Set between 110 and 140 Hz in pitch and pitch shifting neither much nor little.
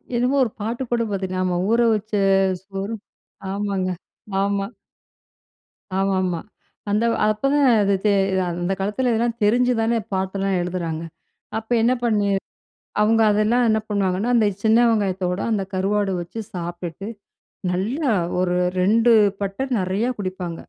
No: high, 200 Hz; average, 3.3 semitones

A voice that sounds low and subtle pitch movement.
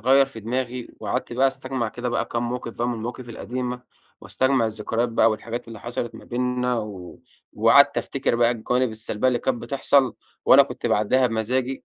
Yes: low, 120 Hz; narrow, 1.9 semitones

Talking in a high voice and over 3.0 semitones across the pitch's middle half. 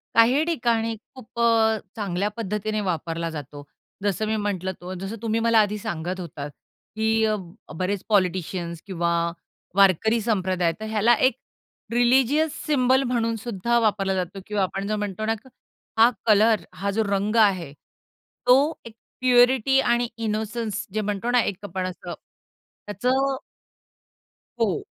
Yes: high, 215 Hz; average, 3.6 semitones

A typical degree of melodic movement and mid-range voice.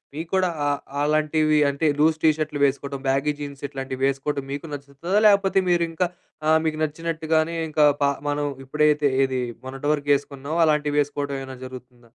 No: narrow, 2.2 semitones; medium, 145 Hz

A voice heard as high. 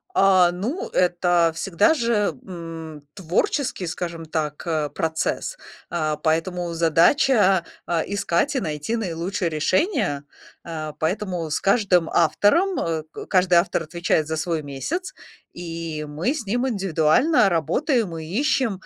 No: medium, 175 Hz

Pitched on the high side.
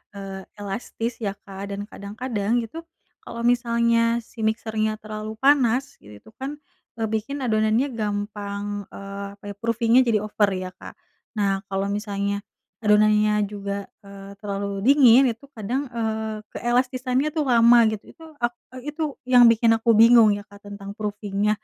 Yes: high, 215 Hz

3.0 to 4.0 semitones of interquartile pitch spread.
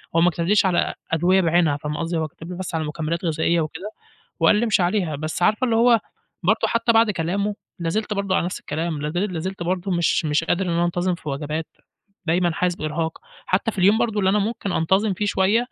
Yes: average, 3.6 semitones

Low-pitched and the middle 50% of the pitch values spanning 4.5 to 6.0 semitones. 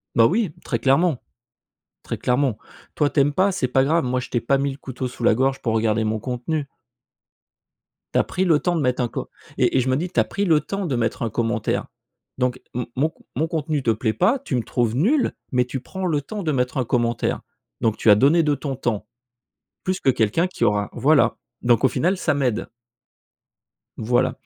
Yes: low, 130 Hz; average, 4.8 semitones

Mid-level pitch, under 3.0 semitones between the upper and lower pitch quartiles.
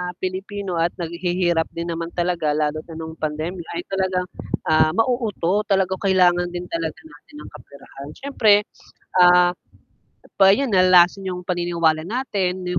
Yes: medium, 180 Hz; narrow, 2.5 semitones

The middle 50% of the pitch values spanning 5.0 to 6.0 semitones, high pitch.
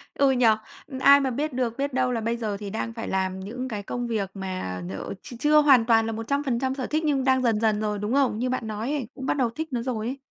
No: average, 3.6 semitones; high, 240 Hz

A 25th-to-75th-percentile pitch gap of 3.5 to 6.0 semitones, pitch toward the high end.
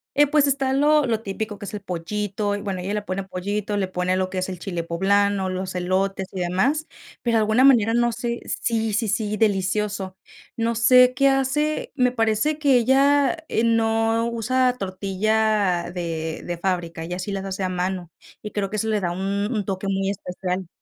Yes: average, 3.8 semitones; high, 205 Hz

